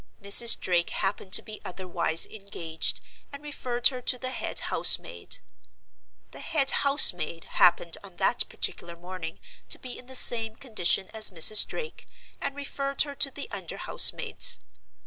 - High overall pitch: Yes, high, 220 Hz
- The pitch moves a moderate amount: No, wide, 7.0 semitones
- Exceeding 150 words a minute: Yes, average, 165 wpm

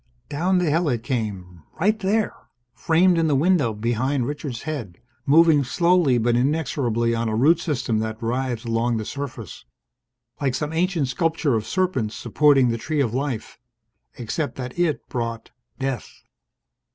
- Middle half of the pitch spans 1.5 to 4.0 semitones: No, wide, 5.5 semitones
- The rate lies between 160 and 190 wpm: No, average, 150 wpm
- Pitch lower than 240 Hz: Yes, low, 135 Hz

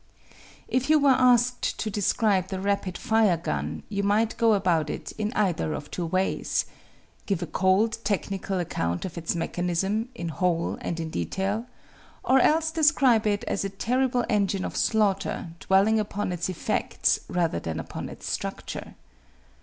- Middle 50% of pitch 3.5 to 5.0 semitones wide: Yes, average, 4.1 semitones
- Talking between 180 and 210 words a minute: No, average, 160 wpm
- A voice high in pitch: Yes, high, 200 Hz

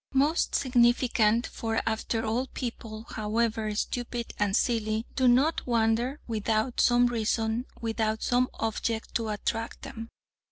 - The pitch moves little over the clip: Yes, narrow, 1.7 semitones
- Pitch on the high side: Yes, high, 230 Hz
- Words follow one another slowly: Yes, slow, 125 wpm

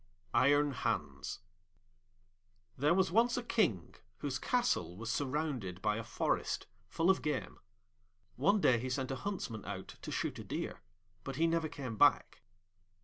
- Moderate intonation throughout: No, wide, 6.7 semitones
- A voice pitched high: No, medium, 140 Hz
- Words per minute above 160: No, average, 150 wpm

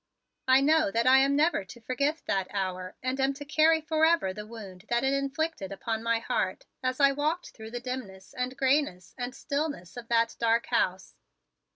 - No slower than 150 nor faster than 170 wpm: No, average, 190 wpm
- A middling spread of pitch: Yes, average, 4.6 semitones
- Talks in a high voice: Yes, very high, 255 Hz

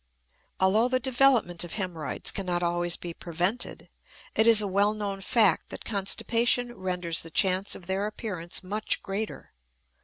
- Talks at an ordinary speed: Yes, average, 150 wpm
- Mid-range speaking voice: No, high, 195 Hz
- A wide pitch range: No, average, 3.8 semitones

